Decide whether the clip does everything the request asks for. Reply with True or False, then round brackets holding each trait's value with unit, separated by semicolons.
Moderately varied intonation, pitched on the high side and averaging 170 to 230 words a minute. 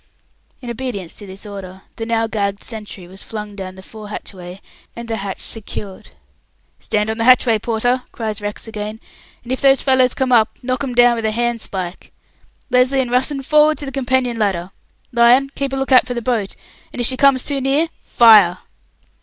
True (3.7 semitones; 230 Hz; 195 wpm)